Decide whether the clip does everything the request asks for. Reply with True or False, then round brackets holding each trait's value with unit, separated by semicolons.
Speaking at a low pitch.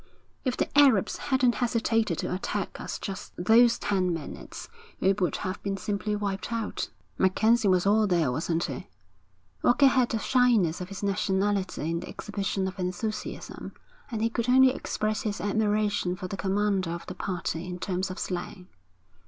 False (200 Hz)